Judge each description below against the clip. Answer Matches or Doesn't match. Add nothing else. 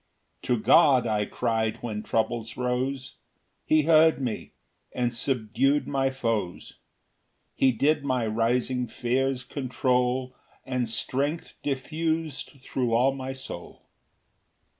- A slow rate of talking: Matches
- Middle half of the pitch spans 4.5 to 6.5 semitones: Doesn't match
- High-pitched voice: Doesn't match